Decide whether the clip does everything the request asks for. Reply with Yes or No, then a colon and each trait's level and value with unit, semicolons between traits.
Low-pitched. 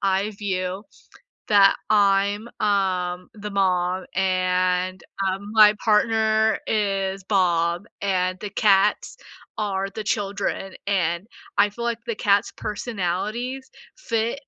No: high, 200 Hz